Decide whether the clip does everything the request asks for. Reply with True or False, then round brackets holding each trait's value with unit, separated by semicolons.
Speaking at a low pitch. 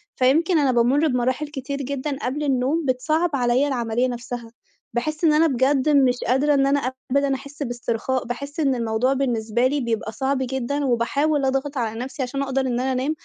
False (265 Hz)